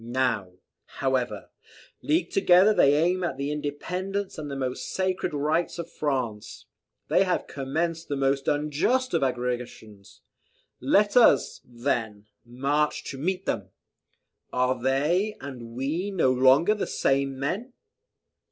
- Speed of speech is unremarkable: No, slow, 130 wpm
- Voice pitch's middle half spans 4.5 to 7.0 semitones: Yes, wide, 5.4 semitones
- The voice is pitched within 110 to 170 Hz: Yes, medium, 140 Hz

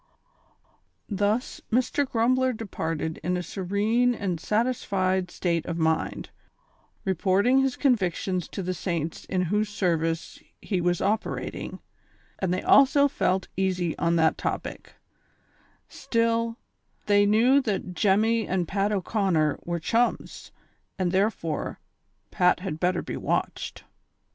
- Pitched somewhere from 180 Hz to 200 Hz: Yes, high, 190 Hz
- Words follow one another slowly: Yes, slow, 120 wpm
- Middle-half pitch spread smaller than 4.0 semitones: No, average, 4.3 semitones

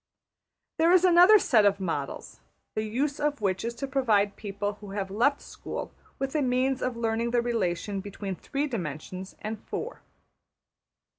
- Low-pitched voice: No, high, 225 Hz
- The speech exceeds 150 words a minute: Yes, average, 160 wpm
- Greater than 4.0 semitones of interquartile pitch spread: Yes, average, 5.2 semitones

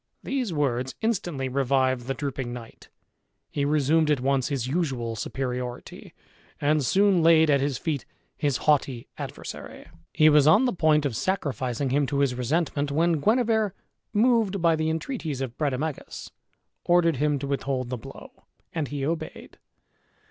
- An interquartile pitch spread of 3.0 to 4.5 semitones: Yes, average, 3.8 semitones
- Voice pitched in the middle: Yes, medium, 145 Hz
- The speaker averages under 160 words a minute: Yes, average, 150 wpm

